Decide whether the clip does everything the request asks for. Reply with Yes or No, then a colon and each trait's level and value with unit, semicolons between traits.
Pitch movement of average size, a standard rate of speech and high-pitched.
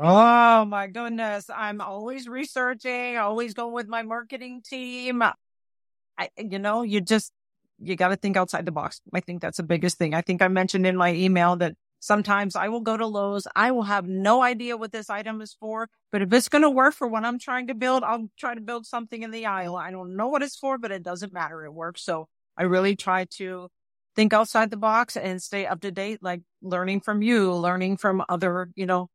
No: average, 4.1 semitones; fast, 225 wpm; high, 205 Hz